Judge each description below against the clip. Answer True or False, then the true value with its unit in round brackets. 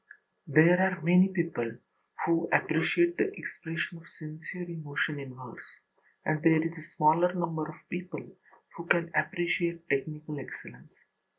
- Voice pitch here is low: False (165 Hz)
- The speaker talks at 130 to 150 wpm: True (135 wpm)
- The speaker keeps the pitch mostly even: True (2.2 semitones)